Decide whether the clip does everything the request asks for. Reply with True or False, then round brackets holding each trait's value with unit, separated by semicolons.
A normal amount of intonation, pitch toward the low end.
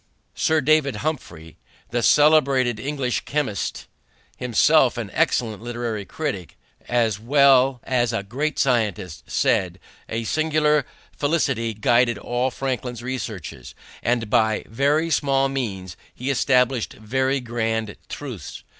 True (3.7 semitones; 125 Hz)